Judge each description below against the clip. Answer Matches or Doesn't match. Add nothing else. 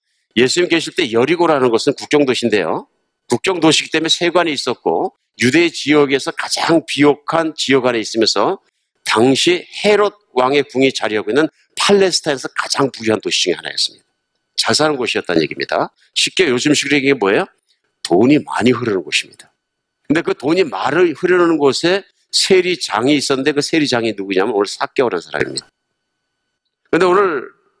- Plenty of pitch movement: Doesn't match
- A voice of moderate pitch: Matches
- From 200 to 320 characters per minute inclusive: Doesn't match